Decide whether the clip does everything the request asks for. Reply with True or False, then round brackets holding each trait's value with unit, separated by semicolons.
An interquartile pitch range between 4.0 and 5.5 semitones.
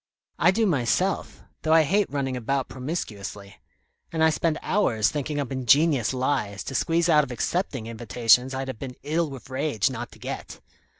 True (4.5 semitones)